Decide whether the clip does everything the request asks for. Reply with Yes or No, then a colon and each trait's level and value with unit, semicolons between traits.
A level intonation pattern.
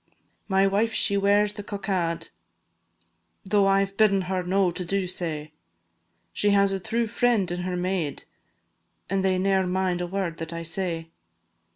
Yes: narrow, 1.9 semitones